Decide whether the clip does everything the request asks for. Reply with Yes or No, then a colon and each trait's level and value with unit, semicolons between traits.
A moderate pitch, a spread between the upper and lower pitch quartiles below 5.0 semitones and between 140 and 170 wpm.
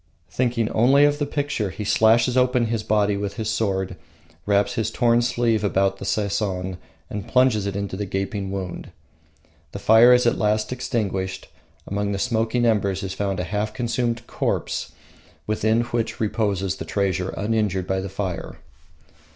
No: low, 105 Hz; average, 3.2 semitones; average, 160 wpm